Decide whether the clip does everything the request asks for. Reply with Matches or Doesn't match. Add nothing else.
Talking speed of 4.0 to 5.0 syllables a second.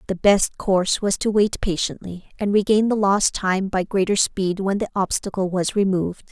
Matches